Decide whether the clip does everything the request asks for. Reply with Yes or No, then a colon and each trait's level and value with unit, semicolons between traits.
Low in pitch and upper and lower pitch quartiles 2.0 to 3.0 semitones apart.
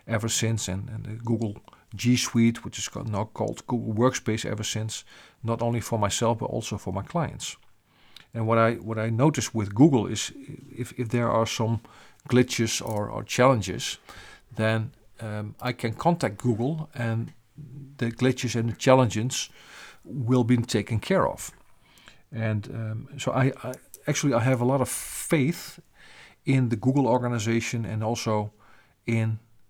Yes: low, 115 Hz; narrow, 2.5 semitones